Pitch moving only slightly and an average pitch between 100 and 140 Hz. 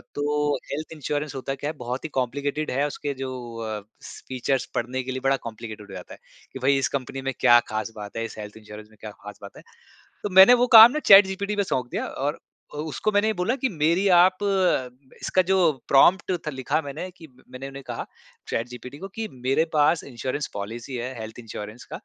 No: average, 4.8 semitones; low, 135 Hz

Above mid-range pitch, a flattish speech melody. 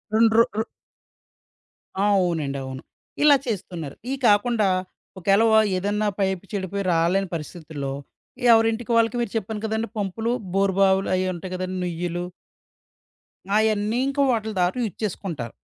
No: high, 195 Hz; average, 3.8 semitones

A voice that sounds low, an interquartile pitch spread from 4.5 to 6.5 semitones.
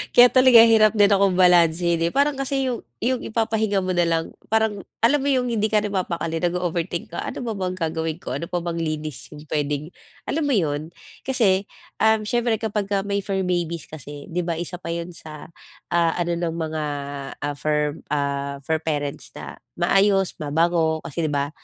No: medium, 175 Hz; average, 5.0 semitones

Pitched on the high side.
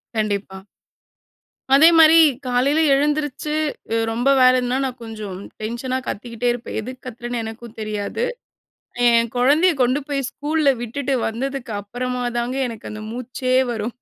Yes: high, 245 Hz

